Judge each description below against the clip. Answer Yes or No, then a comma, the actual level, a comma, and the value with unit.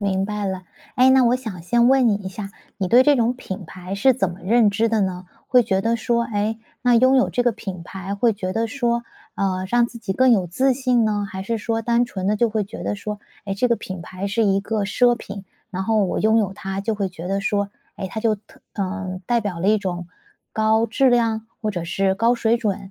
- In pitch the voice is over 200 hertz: Yes, high, 210 Hz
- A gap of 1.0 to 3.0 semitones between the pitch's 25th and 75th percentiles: No, average, 3.4 semitones